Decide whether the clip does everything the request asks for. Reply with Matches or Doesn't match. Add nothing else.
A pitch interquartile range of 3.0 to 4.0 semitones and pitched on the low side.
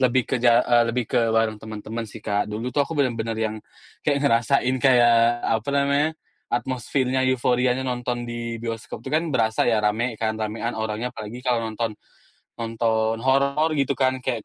Doesn't match